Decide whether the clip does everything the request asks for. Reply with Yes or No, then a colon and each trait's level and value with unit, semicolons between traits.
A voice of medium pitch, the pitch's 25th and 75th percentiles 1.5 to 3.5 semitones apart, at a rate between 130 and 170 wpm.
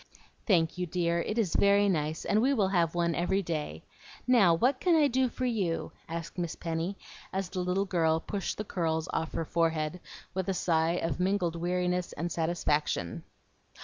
No: medium, 175 Hz; average, 3.2 semitones; average, 180 wpm